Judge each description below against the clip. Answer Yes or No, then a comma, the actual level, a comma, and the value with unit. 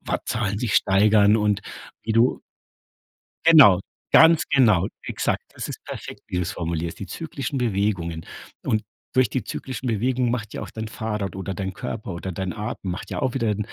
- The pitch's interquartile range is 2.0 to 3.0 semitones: No, average, 4.1 semitones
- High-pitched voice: No, low, 105 Hz